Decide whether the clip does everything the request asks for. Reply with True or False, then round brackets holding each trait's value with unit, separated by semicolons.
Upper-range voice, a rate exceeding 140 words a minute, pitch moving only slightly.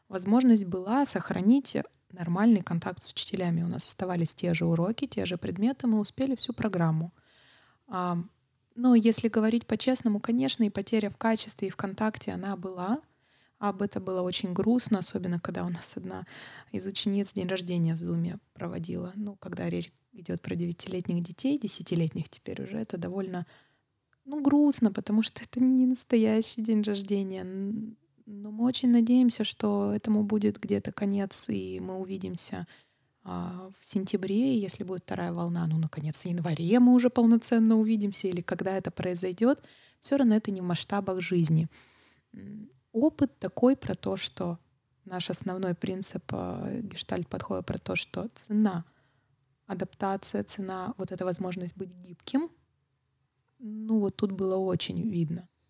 False (195 Hz; 150 wpm; 3.7 semitones)